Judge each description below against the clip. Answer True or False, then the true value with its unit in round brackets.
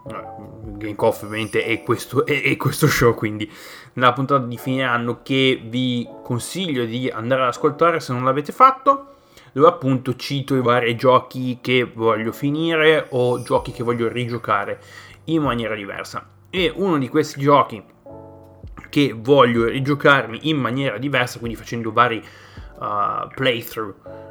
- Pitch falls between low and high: False (125 Hz)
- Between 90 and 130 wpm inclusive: False (145 wpm)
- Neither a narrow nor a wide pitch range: True (4.0 semitones)